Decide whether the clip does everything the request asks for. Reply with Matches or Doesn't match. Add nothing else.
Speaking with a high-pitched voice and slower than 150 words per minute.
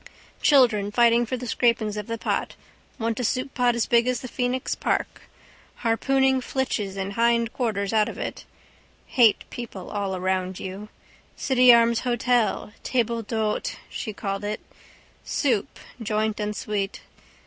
Matches